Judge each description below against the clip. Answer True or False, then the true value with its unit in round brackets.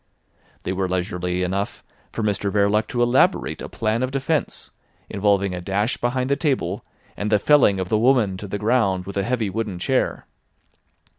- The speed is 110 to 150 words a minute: False (175 wpm)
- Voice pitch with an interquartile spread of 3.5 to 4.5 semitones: True (4.1 semitones)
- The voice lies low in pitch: True (105 Hz)